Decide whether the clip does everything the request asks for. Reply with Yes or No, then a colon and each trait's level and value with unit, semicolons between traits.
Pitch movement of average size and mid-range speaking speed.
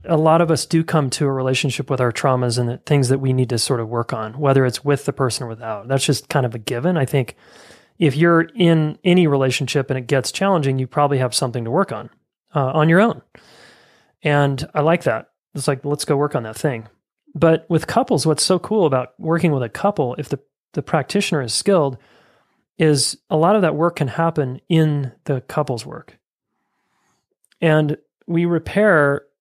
No: average, 3.7 semitones; fast, 210 wpm